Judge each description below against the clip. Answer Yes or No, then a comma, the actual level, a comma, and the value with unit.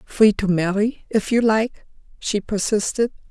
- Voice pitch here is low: No, high, 210 Hz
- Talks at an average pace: Yes, average, 145 wpm